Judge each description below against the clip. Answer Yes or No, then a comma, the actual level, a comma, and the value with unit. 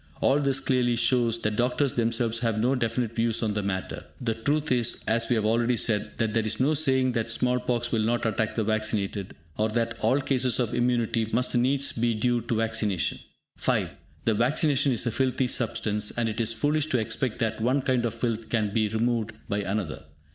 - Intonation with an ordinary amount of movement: No, narrow, 2.3 semitones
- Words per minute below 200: No, fast, 205 wpm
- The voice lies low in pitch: Yes, low, 115 Hz